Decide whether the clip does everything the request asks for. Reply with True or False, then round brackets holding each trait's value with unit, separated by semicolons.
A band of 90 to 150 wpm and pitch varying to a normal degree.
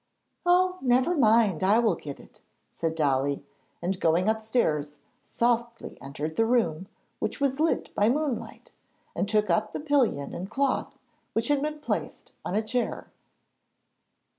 False (145 wpm; 7.4 semitones)